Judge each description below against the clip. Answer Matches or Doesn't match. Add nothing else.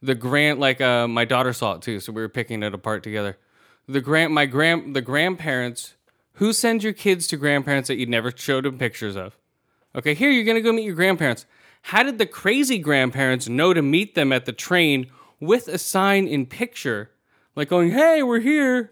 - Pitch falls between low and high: Matches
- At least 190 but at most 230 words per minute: Matches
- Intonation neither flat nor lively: Doesn't match